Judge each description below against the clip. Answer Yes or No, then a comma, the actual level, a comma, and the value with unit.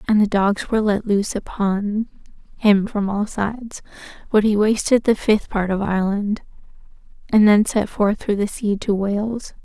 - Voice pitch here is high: Yes, high, 205 Hz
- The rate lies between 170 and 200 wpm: Yes, average, 175 wpm